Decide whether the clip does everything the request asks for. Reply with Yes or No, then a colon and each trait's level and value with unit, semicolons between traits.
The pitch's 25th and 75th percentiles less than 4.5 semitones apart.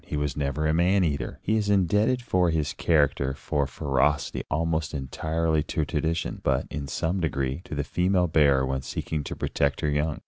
Yes: average, 3.0 semitones